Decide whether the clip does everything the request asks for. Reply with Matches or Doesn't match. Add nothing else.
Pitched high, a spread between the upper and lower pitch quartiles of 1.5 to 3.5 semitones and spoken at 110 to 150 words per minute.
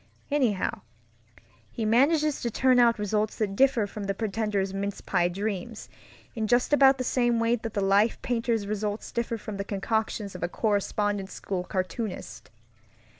Doesn't match